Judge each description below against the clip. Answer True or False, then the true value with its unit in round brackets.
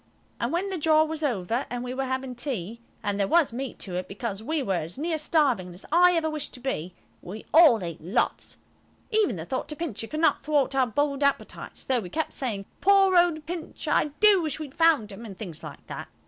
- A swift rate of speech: True (215 wpm)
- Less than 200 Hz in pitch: False (270 Hz)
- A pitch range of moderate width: False (6.9 semitones)